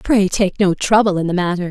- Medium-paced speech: No, fast, 245 wpm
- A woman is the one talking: Yes, female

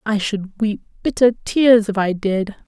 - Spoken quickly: No, average, 180 wpm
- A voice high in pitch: Yes, high, 210 Hz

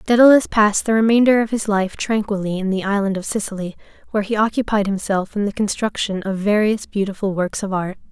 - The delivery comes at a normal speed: Yes, average, 190 wpm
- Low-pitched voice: No, high, 205 Hz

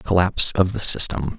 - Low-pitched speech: Yes, very low, 90 Hz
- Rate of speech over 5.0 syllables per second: Yes, 5.2 syllables/s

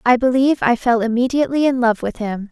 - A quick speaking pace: Yes, fast, 215 wpm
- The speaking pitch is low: No, high, 245 Hz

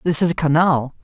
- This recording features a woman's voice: No, male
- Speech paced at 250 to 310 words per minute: No, fast, 230 wpm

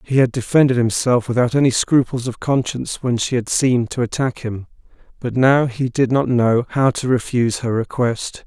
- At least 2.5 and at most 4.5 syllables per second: No, 5.1 syllables/s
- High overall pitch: No, low, 125 Hz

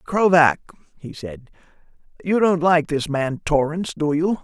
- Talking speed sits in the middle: Yes, average, 150 wpm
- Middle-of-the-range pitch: Yes, medium, 160 Hz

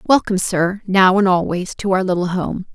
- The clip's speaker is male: No, female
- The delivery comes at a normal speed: Yes, average, 195 wpm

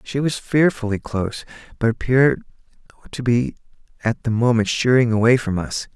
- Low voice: Yes, low, 120 Hz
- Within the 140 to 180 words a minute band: Yes, average, 150 wpm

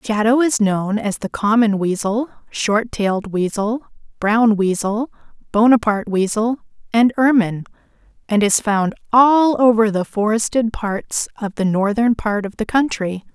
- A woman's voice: Yes, female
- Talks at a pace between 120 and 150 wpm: Yes, average, 140 wpm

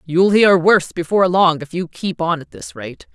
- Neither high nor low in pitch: Yes, medium, 175 Hz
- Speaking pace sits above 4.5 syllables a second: Yes, 5.0 syllables/s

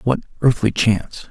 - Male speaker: Yes, male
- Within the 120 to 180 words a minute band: Yes, average, 140 wpm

